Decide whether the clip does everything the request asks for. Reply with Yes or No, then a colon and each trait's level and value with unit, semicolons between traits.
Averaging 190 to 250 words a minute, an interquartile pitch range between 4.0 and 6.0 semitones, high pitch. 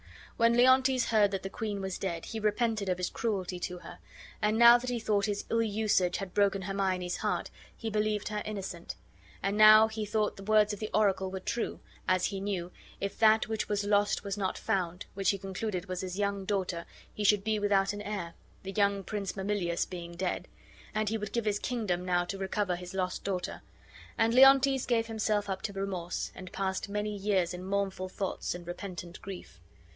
No: average, 200 wpm; narrow, 2.4 semitones; high, 200 Hz